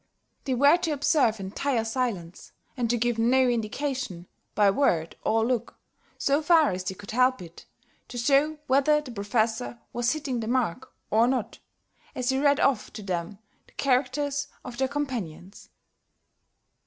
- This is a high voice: Yes, high, 245 Hz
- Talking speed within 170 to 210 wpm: No, average, 155 wpm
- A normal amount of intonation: Yes, average, 4.2 semitones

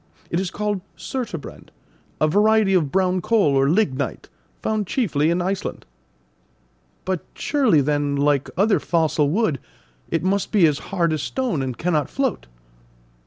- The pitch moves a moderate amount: No, wide, 5.8 semitones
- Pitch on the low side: No, medium, 180 Hz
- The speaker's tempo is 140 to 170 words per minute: Yes, average, 145 wpm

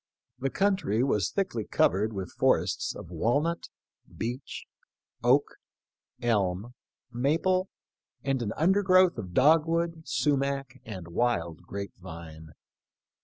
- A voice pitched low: Yes, low, 125 Hz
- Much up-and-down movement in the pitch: Yes, wide, 8.4 semitones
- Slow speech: Yes, slow, 115 wpm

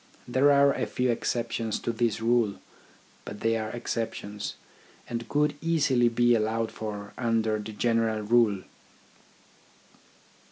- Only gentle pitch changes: Yes, narrow, 1.8 semitones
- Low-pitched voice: Yes, low, 115 Hz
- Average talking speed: No, slow, 125 wpm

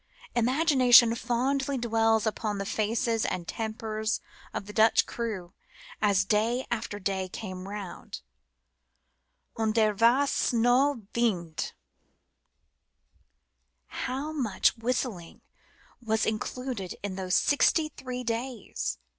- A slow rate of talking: Yes, slow, 105 wpm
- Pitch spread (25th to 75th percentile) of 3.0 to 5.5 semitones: Yes, average, 3.3 semitones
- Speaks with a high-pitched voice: Yes, high, 225 Hz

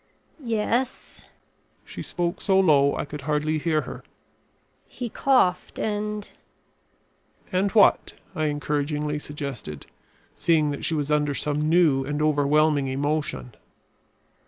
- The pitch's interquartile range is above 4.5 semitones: No, average, 3.3 semitones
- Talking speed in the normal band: No, slow, 120 wpm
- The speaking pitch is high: No, medium, 150 Hz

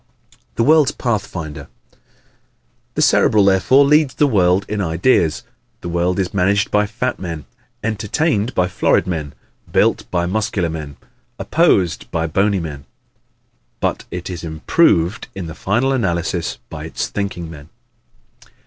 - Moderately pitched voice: No, very low, 95 Hz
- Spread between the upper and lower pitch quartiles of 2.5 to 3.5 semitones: No, average, 4.4 semitones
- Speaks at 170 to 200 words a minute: No, slow, 135 wpm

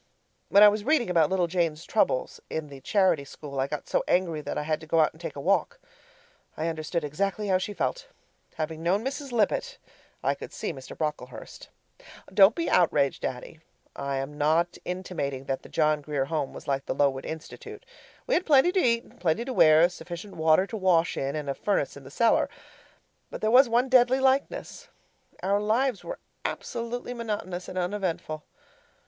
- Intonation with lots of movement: Yes, wide, 6.5 semitones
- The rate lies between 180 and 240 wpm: Yes, average, 190 wpm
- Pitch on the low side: No, medium, 175 Hz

